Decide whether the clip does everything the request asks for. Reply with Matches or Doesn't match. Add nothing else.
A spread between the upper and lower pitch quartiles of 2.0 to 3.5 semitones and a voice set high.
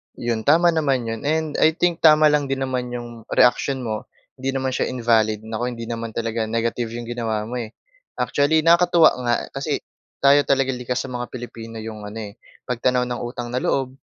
Doesn't match